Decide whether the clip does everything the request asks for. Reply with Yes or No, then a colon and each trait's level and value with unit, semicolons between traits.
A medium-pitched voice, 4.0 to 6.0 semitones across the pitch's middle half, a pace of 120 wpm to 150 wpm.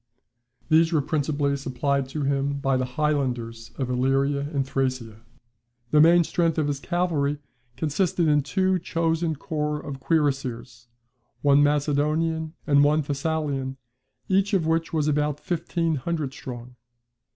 No: medium, 145 Hz; average, 2.9 semitones; slow, 135 wpm